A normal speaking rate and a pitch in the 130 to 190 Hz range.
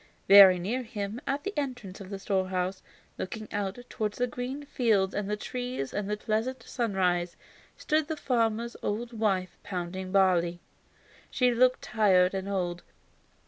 No: average, 150 wpm; high, 205 Hz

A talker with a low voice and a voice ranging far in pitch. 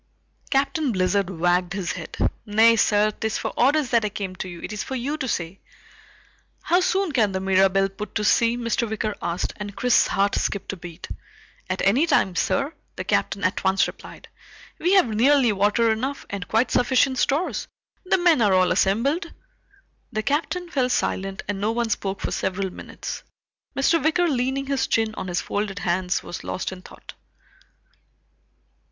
No: high, 215 Hz; wide, 5.7 semitones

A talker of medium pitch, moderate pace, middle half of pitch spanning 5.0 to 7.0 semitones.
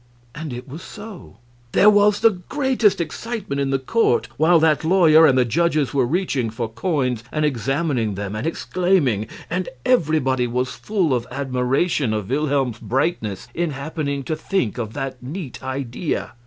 Yes: medium, 145 Hz; average, 160 wpm; wide, 5.5 semitones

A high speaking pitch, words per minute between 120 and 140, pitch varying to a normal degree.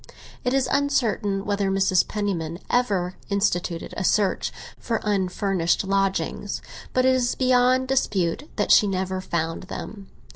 Yes: high, 200 Hz; slow, 135 wpm; average, 4.8 semitones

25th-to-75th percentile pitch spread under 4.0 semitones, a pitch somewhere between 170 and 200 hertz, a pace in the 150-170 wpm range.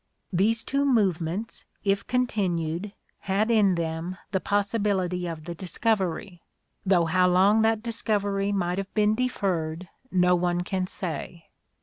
No: average, 3.1 semitones; high, 190 Hz; slow, 135 wpm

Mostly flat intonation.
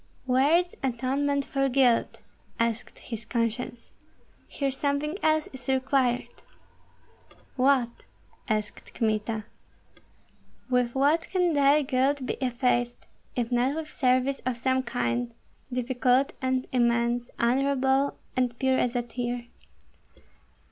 Yes: narrow, 2.3 semitones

